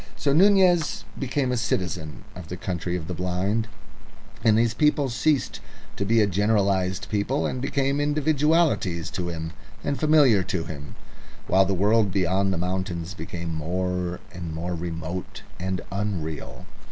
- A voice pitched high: No, very low, 95 Hz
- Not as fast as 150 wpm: Yes, average, 140 wpm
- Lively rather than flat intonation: Yes, wide, 6.2 semitones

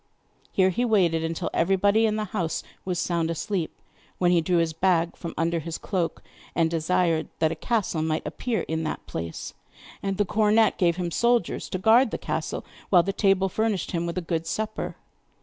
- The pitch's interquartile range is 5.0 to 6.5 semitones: No, average, 3.9 semitones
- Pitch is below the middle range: No, medium, 180 Hz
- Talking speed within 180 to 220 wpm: Yes, average, 190 wpm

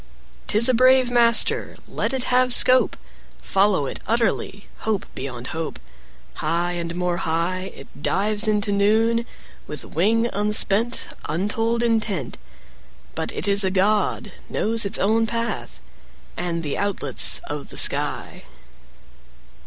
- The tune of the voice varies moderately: Yes, average, 4.5 semitones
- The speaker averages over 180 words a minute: No, slow, 135 wpm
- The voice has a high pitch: Yes, high, 205 Hz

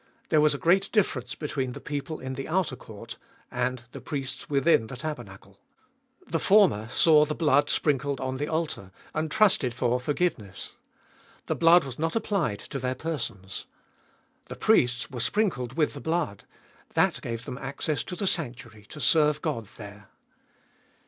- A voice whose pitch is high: No, medium, 140 Hz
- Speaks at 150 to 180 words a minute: Yes, average, 165 wpm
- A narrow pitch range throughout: No, average, 4.6 semitones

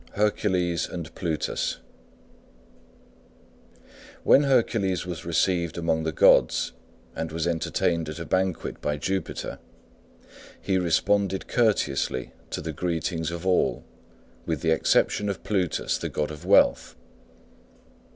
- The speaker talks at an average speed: No, slow, 115 wpm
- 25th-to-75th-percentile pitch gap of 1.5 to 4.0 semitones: Yes, average, 2.8 semitones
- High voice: No, very low, 85 Hz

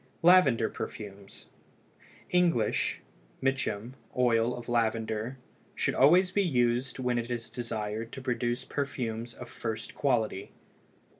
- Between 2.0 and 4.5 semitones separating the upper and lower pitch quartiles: Yes, average, 2.8 semitones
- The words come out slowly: Yes, slow, 115 wpm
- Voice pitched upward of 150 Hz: No, low, 120 Hz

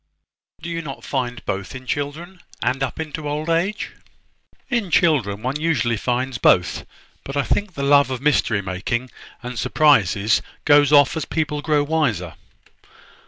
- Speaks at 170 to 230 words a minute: No, average, 155 wpm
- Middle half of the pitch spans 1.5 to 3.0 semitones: No, average, 4.3 semitones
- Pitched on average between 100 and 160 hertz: Yes, medium, 140 Hz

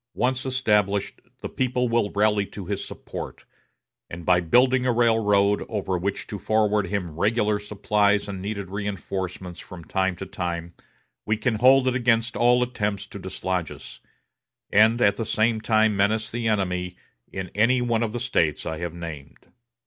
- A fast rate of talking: No, average, 165 wpm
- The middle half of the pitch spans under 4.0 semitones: Yes, average, 3.4 semitones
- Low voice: Yes, low, 105 Hz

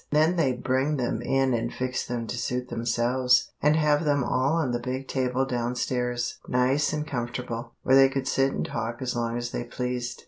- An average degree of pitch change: No, narrow, 1.9 semitones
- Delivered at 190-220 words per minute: Yes, fast, 205 wpm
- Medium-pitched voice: No, low, 125 Hz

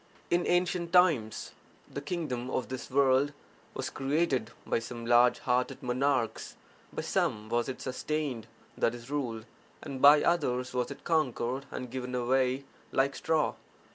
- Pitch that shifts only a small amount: No, average, 3.0 semitones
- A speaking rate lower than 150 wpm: Yes, average, 140 wpm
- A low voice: Yes, low, 130 Hz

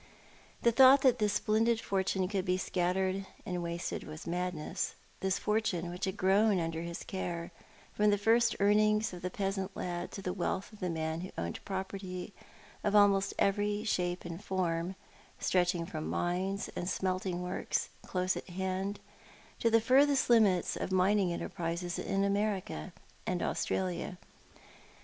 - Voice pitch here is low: No, high, 190 Hz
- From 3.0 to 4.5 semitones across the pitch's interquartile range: No, narrow, 2.6 semitones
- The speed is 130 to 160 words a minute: Yes, average, 155 wpm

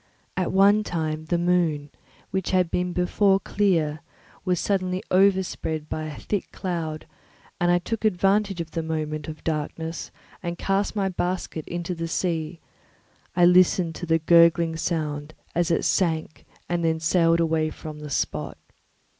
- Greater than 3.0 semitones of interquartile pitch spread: No, narrow, 2.5 semitones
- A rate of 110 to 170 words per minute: Yes, average, 155 wpm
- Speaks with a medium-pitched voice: Yes, medium, 170 Hz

